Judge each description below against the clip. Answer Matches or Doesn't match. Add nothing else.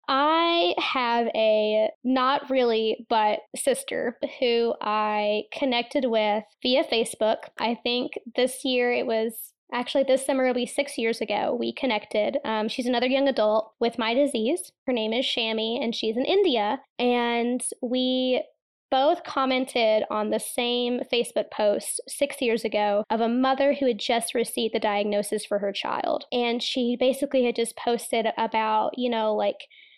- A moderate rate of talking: Matches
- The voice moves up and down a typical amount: Matches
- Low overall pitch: Doesn't match